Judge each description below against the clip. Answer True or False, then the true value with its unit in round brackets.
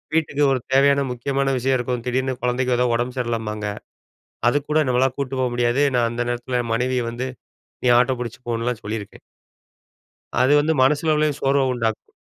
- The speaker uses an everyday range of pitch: False (2.2 semitones)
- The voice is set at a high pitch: False (125 Hz)